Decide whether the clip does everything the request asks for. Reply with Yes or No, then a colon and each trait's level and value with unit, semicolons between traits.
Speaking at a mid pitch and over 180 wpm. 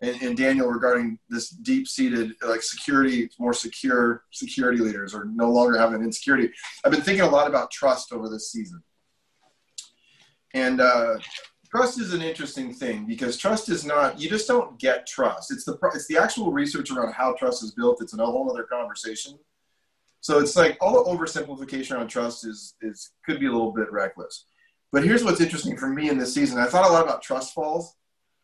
Yes: medium, 150 Hz; average, 190 wpm